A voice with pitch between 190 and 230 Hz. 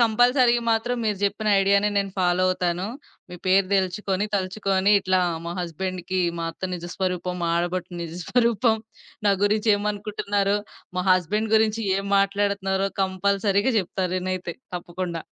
Yes: high, 195 Hz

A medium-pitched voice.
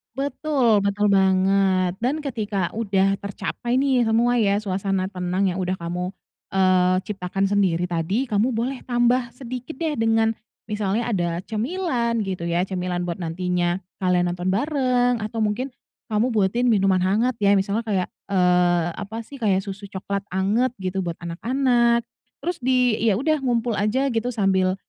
No: high, 205 Hz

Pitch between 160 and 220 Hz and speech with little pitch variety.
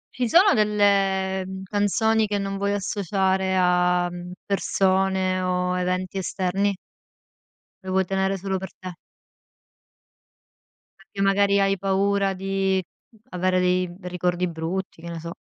Yes: high, 190 Hz; narrow, 1.4 semitones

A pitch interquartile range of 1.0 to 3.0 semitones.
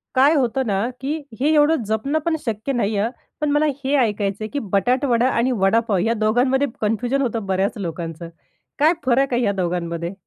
No: average, 5.2 semitones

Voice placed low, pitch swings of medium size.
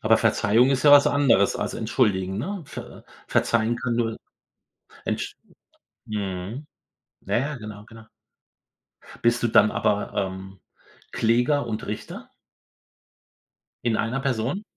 Yes: low, 115 Hz; average, 3.7 semitones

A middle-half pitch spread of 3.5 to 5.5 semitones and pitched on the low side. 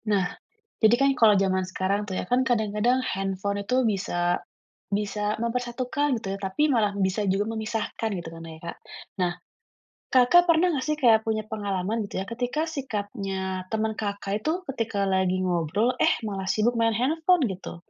No: average, 4.1 semitones; high, 210 Hz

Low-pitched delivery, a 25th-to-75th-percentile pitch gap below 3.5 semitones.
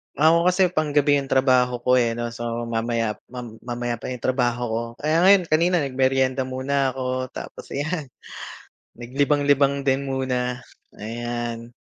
Yes: low, 130 Hz; average, 2.9 semitones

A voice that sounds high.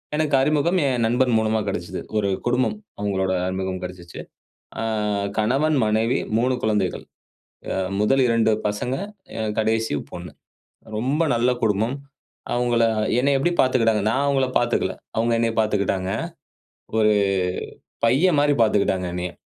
No: low, 115 Hz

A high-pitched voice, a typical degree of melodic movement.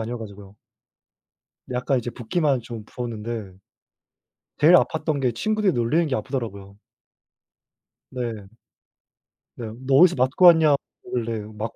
No: low, 120 Hz; average, 4.6 semitones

